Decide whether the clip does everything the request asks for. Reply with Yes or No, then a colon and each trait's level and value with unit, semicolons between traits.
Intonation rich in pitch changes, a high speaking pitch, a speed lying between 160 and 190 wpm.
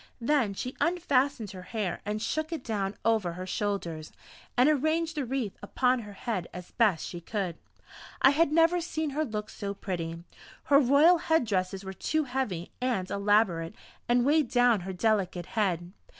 Yes: wide, 6.7 semitones; high, 220 Hz; average, 170 wpm